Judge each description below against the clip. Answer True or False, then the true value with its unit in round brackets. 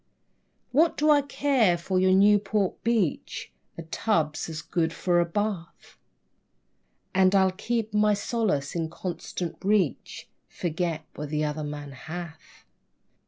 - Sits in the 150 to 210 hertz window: True (185 Hz)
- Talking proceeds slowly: True (130 wpm)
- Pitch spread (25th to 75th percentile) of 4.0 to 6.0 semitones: True (4.7 semitones)